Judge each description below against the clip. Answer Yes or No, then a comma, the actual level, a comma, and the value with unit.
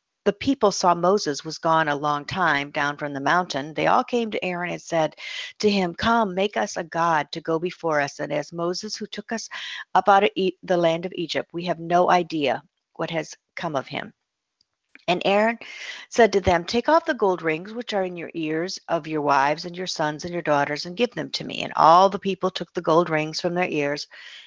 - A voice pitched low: No, medium, 175 Hz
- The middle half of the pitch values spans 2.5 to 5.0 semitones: Yes, average, 3.9 semitones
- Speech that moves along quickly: Yes, fast, 230 wpm